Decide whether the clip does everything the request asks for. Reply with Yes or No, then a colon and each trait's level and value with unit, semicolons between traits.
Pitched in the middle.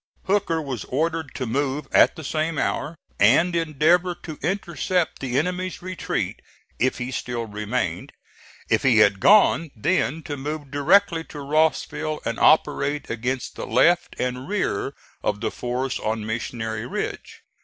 Yes: medium, 145 Hz